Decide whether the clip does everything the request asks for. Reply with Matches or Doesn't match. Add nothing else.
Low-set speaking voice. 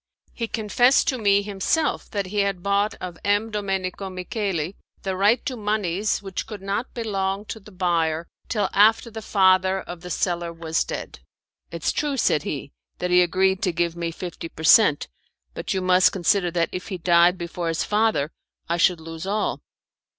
Doesn't match